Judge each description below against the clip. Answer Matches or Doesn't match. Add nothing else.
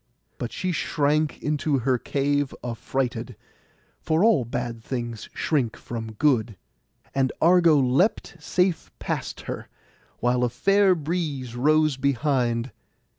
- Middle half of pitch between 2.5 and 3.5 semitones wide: Doesn't match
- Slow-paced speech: Matches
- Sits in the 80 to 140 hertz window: Matches